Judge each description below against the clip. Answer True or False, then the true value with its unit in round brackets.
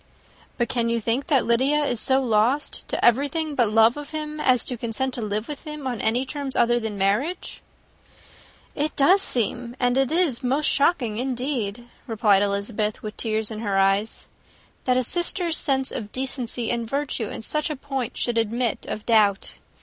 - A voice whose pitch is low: False (245 Hz)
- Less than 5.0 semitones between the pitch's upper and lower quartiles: True (4.0 semitones)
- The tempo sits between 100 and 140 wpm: False (180 wpm)